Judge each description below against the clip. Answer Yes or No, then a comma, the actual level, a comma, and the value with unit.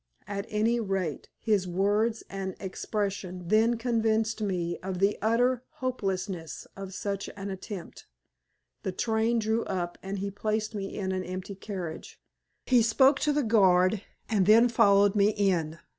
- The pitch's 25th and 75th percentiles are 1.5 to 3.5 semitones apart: Yes, average, 2.8 semitones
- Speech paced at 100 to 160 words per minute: Yes, average, 150 wpm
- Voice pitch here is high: Yes, high, 200 Hz